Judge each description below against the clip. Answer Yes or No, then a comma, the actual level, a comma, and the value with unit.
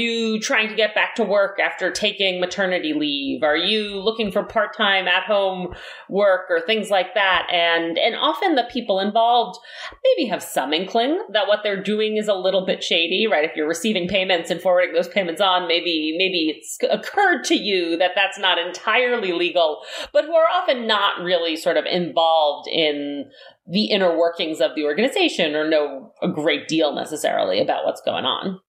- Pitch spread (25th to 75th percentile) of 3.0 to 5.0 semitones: Yes, average, 4.2 semitones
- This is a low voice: No, high, 195 Hz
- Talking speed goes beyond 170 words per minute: Yes, average, 190 wpm